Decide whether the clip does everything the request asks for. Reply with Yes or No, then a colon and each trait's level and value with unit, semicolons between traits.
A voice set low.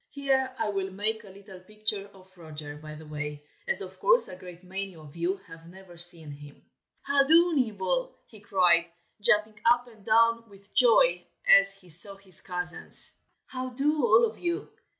No: high, 195 Hz